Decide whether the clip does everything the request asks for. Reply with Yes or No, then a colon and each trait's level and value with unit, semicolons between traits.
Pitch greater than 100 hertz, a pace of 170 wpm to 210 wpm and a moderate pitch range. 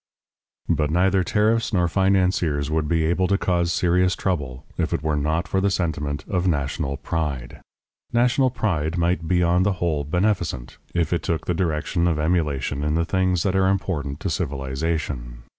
No: very low, 85 Hz; average, 175 wpm; average, 3.7 semitones